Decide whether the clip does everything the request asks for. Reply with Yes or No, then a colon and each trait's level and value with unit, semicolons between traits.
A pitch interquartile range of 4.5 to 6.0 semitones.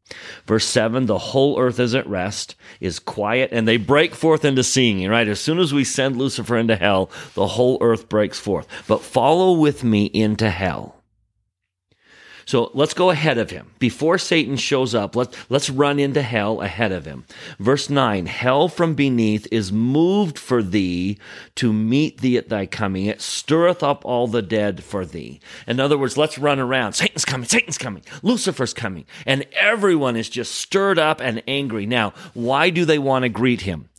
Yes: average, 4.9 semitones